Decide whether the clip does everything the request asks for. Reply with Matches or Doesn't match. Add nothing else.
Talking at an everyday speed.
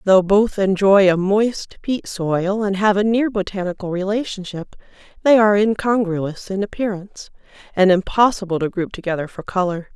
Matches